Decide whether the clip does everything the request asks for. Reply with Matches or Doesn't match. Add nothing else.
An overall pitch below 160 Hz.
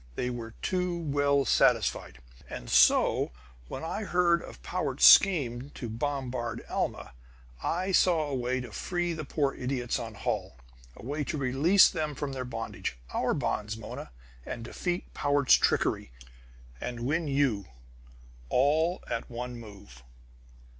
Matches